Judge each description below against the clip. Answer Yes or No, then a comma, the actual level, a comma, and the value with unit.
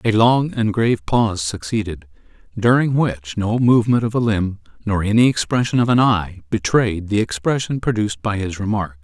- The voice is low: Yes, low, 105 Hz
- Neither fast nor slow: Yes, average, 175 wpm